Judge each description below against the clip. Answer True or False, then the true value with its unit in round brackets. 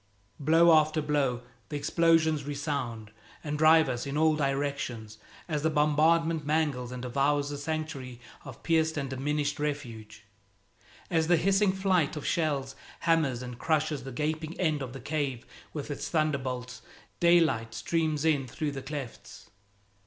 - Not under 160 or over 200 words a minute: False (145 wpm)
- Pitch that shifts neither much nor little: True (3.0 semitones)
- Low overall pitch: False (150 Hz)